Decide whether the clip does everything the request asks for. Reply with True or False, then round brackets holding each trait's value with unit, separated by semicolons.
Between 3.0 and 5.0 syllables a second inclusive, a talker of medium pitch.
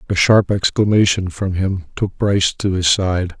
False (4.5 syllables/s; 95 Hz)